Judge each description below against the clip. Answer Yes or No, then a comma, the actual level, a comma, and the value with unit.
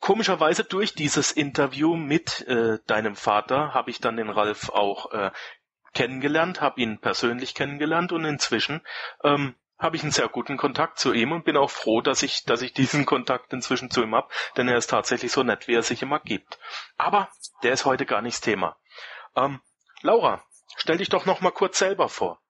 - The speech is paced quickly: Yes, fast, 195 wpm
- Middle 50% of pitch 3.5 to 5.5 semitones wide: Yes, average, 4.3 semitones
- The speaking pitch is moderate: Yes, medium, 145 Hz